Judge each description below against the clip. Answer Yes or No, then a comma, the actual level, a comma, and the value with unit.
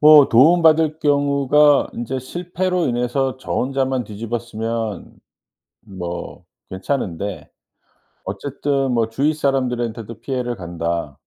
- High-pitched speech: No, low, 125 Hz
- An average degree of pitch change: Yes, average, 4.4 semitones